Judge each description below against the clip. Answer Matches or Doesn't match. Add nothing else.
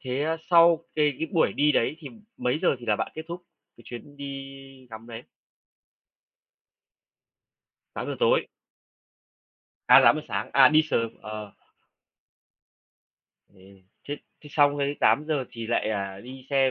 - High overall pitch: Doesn't match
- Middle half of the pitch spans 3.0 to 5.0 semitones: Matches